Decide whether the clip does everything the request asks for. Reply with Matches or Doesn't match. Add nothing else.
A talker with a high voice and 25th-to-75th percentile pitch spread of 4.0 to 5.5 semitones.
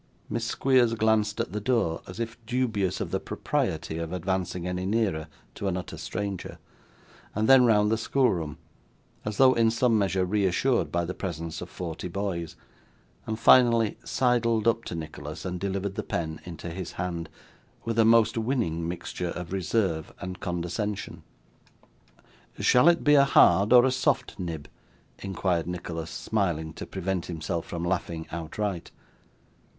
Doesn't match